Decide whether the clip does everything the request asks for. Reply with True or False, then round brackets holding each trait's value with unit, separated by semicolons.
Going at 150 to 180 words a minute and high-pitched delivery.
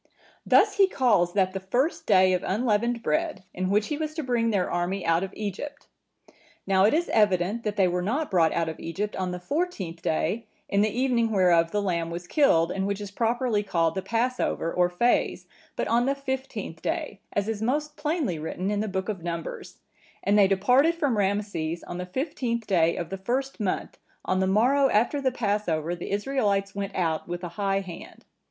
False (200 wpm; 205 Hz)